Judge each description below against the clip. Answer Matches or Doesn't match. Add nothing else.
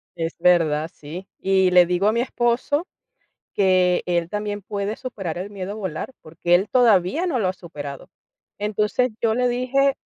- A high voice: Matches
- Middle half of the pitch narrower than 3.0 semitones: Doesn't match